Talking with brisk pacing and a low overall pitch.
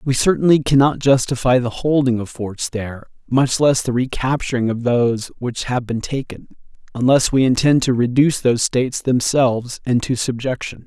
No: average, 165 wpm; low, 125 Hz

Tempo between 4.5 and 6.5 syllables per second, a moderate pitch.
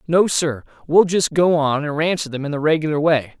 Yes: 5.4 syllables/s; medium, 155 Hz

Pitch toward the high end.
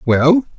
No: medium, 165 Hz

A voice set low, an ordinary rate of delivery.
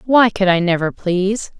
No: high, 195 Hz; average, 190 wpm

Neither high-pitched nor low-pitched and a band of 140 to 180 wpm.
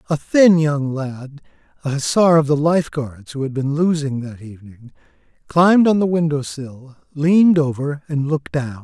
Yes: medium, 145 Hz; average, 175 wpm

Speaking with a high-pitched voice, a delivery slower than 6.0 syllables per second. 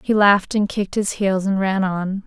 Yes: high, 195 Hz; 5.1 syllables/s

